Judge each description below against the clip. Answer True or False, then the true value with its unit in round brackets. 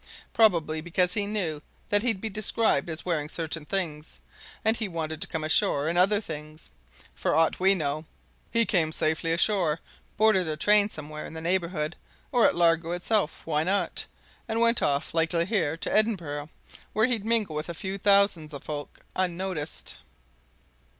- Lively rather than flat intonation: False (4.4 semitones)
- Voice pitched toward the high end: False (170 Hz)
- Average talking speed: True (170 wpm)